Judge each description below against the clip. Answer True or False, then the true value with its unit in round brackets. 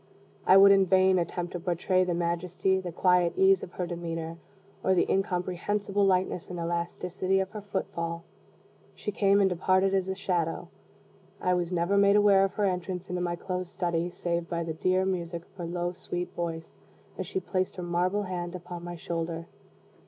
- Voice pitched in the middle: True (180 Hz)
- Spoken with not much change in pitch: True (1.7 semitones)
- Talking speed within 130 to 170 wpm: False (185 wpm)